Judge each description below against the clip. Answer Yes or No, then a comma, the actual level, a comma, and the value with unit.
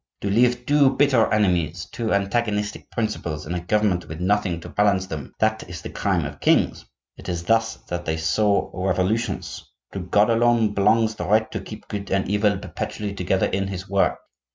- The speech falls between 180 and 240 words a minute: Yes, average, 185 wpm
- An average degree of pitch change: Yes, average, 3.4 semitones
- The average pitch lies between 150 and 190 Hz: No, low, 100 Hz